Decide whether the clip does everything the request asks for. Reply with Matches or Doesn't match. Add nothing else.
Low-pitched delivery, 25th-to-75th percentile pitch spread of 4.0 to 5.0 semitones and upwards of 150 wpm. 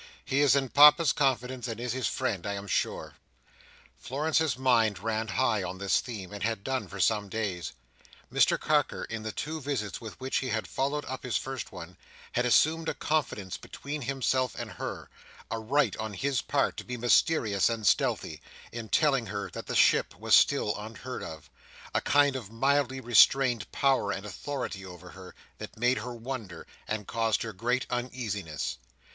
Matches